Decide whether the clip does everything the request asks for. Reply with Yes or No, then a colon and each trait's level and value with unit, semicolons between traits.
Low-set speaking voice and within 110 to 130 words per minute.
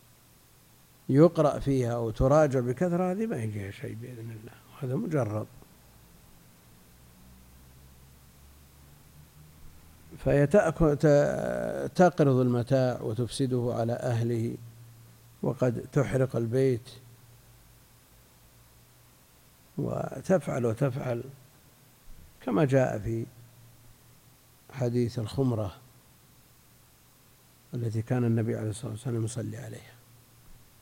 No: low, 120 Hz; average, 70 wpm